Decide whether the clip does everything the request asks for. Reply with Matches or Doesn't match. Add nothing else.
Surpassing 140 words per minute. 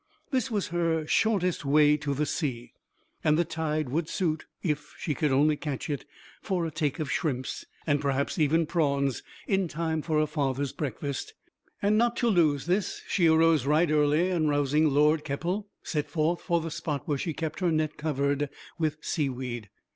Matches